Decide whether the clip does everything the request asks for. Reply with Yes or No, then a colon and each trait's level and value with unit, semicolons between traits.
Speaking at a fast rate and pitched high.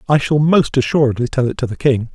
No: fast, 250 wpm; low, 135 Hz